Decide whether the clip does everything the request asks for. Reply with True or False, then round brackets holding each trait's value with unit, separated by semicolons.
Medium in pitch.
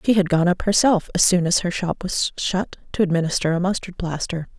True (180 Hz)